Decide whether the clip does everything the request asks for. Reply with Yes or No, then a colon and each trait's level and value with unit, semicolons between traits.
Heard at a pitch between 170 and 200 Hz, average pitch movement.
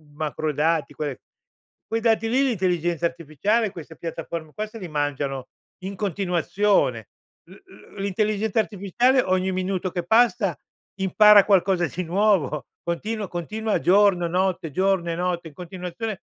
Yes: medium, 185 Hz; average, 3.9 semitones